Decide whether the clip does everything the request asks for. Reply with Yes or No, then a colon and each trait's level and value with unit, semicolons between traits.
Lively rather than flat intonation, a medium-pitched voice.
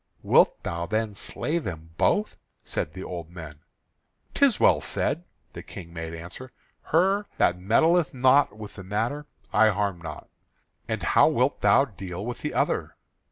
No: wide, 8.5 semitones; low, 105 Hz